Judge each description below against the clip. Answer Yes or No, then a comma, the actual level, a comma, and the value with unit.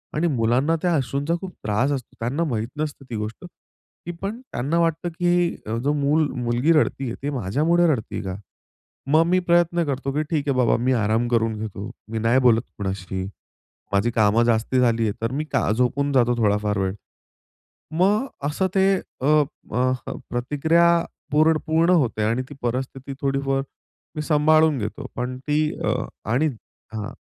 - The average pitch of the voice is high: No, low, 135 Hz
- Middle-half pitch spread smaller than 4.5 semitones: No, average, 5.3 semitones